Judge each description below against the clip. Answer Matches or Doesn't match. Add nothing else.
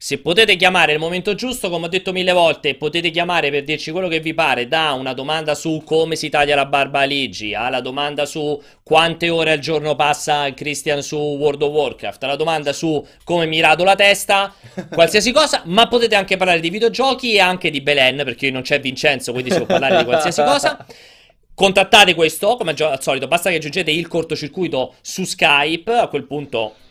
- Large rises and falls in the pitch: Doesn't match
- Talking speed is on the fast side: Matches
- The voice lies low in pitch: Doesn't match